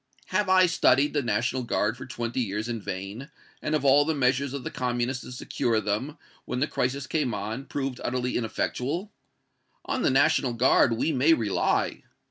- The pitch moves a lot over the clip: No, average, 3.4 semitones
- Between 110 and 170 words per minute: No, average, 180 wpm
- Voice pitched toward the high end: No, low, 125 Hz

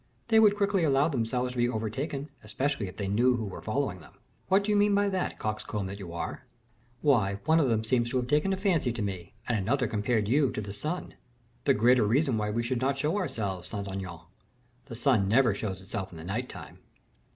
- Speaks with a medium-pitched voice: No, low, 120 Hz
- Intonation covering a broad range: Yes, wide, 5.7 semitones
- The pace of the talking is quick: Yes, fast, 225 wpm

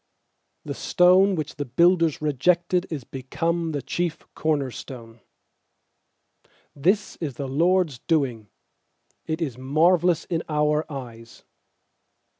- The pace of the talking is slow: Yes, slow, 105 wpm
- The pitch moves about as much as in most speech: Yes, average, 4.4 semitones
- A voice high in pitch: No, medium, 155 Hz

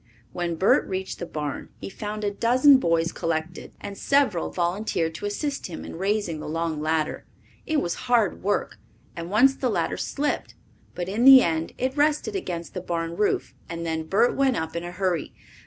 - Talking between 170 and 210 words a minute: Yes, average, 190 wpm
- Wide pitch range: Yes, wide, 6.2 semitones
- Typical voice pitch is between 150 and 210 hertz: Yes, medium, 185 Hz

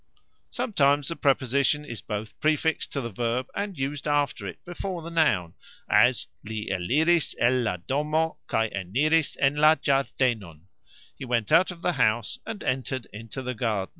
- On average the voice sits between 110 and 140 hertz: Yes, low, 135 Hz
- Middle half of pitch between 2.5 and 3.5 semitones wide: No, average, 5.2 semitones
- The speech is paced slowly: No, average, 165 wpm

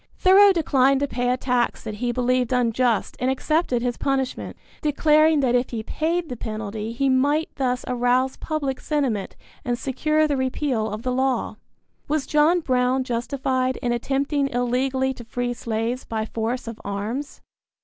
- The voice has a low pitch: No, very high, 255 Hz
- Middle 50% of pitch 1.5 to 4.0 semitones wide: Yes, average, 2.7 semitones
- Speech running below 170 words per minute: Yes, average, 160 wpm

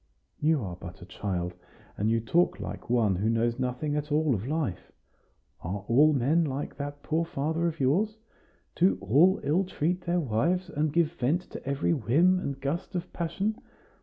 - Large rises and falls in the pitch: Yes, wide, 6.3 semitones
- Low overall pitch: No, medium, 145 Hz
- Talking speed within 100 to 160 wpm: No, average, 180 wpm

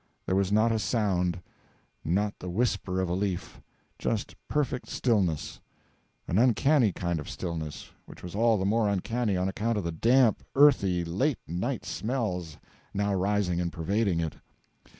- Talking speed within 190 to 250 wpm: No, average, 155 wpm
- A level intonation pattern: No, average, 4.3 semitones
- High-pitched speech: No, low, 100 Hz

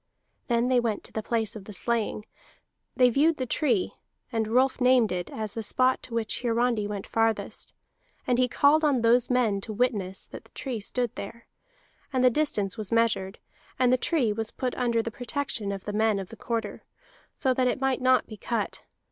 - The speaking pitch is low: No, high, 235 Hz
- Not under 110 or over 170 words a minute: No, average, 200 wpm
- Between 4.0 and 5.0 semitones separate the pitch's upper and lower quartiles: No, average, 2.8 semitones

